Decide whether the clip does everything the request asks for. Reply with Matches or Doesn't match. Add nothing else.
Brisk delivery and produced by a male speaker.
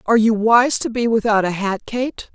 Doesn't match